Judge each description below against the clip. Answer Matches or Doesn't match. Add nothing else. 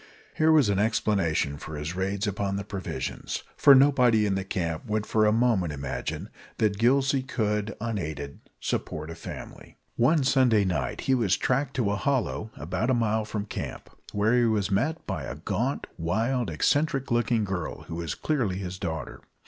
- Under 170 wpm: Doesn't match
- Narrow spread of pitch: Doesn't match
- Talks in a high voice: Doesn't match